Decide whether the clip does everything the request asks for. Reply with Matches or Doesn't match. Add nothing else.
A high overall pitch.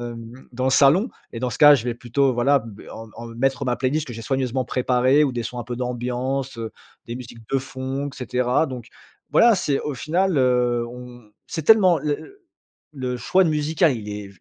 Doesn't match